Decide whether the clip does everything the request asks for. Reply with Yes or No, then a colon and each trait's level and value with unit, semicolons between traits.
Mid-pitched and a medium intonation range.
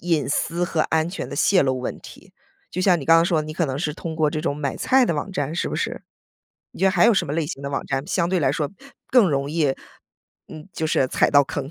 Yes: medium, 155 Hz; average, 3.3 semitones